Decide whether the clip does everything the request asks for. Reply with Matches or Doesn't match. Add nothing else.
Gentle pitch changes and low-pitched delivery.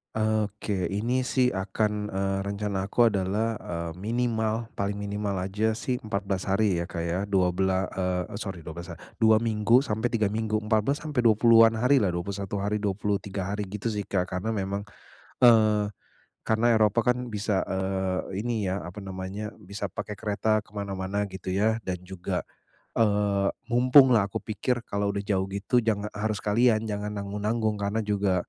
Matches